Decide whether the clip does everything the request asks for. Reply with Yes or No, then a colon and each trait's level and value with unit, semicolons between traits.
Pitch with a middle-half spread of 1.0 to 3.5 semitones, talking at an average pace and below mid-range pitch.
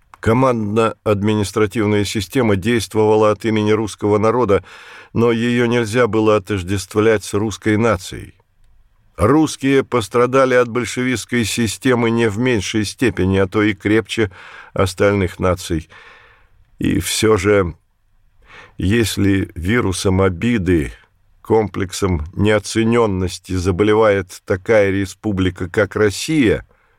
No: average, 2.7 semitones; slow, 95 wpm; low, 105 Hz